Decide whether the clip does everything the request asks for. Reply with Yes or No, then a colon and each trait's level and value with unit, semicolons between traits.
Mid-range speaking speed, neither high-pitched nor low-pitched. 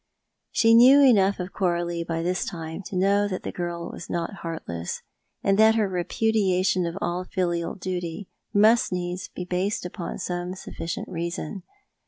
Yes: average, 160 wpm; medium, 180 Hz